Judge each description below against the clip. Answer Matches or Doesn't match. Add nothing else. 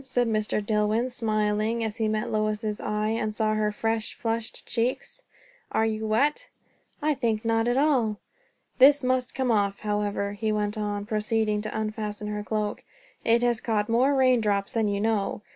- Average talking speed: Matches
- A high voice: Matches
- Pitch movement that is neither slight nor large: Doesn't match